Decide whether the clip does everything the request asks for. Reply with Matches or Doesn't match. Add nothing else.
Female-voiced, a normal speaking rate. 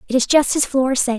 Doesn't match